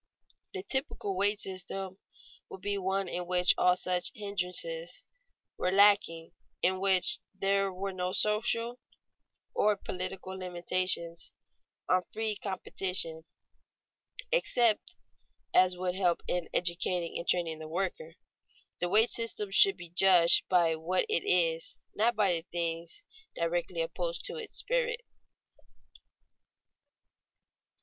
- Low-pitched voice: No, high, 190 Hz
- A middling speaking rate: No, slow, 120 wpm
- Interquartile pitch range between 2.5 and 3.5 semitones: Yes, average, 3.1 semitones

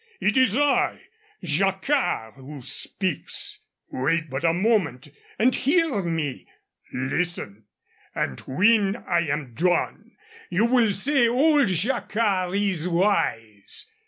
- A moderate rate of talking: No, slow, 110 wpm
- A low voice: No, medium, 185 Hz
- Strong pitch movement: Yes, wide, 7.6 semitones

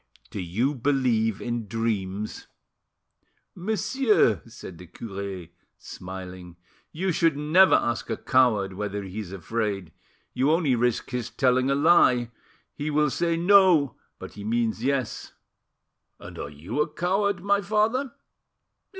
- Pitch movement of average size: No, wide, 8.2 semitones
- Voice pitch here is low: Yes, low, 125 Hz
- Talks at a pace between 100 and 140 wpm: Yes, slow, 135 wpm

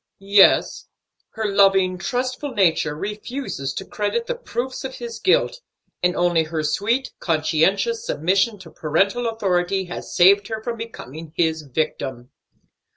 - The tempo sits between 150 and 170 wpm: No, slow, 135 wpm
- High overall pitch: Yes, high, 195 Hz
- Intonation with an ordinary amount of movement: No, wide, 6.1 semitones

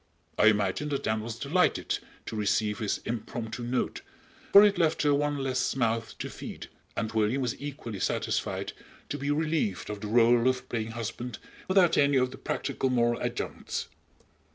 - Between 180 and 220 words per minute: No, average, 170 wpm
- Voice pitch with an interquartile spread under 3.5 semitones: No, average, 4.4 semitones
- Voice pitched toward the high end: No, low, 120 Hz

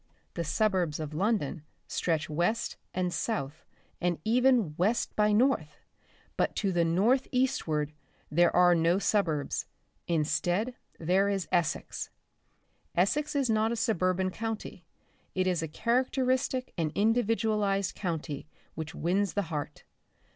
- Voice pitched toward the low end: No, medium, 185 Hz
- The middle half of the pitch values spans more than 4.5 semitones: Yes, average, 5.2 semitones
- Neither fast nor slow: No, slow, 125 wpm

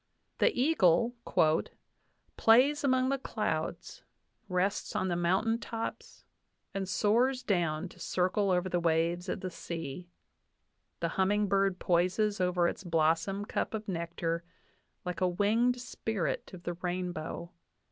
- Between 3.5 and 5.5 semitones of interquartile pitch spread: Yes, average, 4.0 semitones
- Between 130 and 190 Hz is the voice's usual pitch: Yes, medium, 185 Hz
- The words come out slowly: Yes, slow, 130 wpm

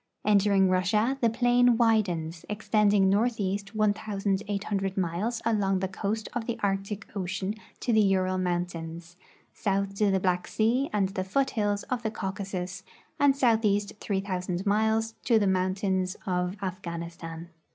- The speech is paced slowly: No, average, 145 wpm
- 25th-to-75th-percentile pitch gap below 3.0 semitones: Yes, narrow, 2.6 semitones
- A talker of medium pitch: No, high, 200 Hz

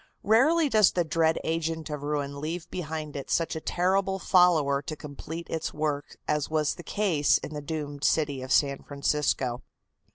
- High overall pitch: No, medium, 155 Hz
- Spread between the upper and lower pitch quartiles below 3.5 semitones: Yes, average, 3.1 semitones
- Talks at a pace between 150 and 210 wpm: Yes, average, 170 wpm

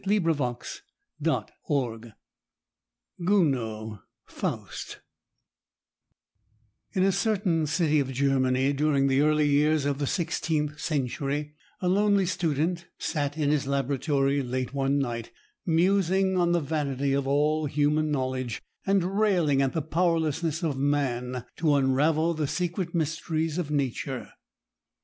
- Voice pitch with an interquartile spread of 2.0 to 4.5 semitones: Yes, average, 3.5 semitones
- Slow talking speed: Yes, slow, 115 wpm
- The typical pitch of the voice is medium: Yes, medium, 150 Hz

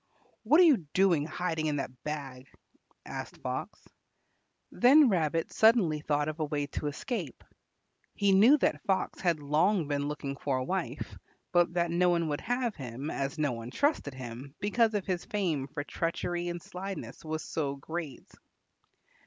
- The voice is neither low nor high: Yes, medium, 160 Hz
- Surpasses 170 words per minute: No, average, 160 wpm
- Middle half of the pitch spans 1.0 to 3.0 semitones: No, average, 4.9 semitones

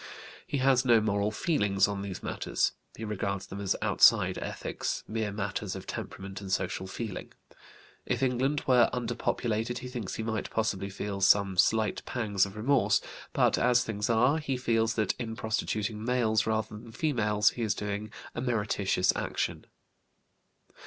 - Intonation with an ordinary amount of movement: Yes, average, 3.1 semitones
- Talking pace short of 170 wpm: Yes, average, 160 wpm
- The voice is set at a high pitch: No, low, 110 Hz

